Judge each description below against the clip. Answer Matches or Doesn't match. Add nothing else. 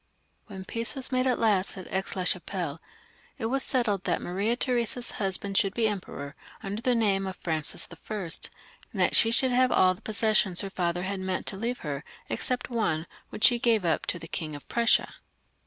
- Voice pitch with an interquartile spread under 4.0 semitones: Doesn't match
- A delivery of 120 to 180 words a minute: Doesn't match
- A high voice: Matches